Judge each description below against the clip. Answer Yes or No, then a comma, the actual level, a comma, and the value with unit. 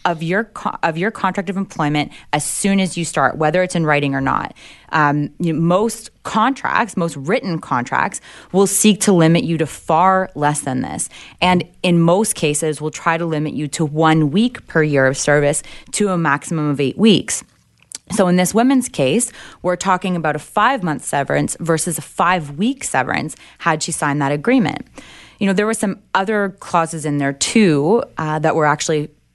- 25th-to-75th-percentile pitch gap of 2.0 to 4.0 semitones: No, average, 4.5 semitones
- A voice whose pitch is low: No, medium, 165 Hz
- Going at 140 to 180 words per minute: No, average, 195 wpm